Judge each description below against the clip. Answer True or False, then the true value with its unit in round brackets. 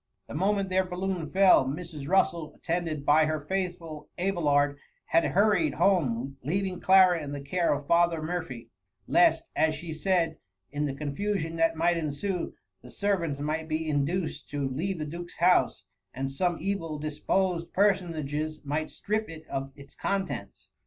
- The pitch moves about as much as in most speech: True (3.8 semitones)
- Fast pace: False (160 wpm)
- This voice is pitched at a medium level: True (165 Hz)